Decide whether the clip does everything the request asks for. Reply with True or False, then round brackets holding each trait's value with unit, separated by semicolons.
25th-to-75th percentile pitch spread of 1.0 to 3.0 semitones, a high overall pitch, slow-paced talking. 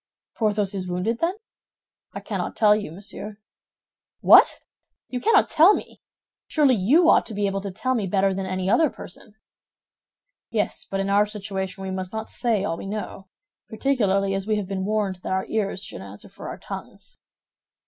False (2.4 semitones; 200 Hz; 180 wpm)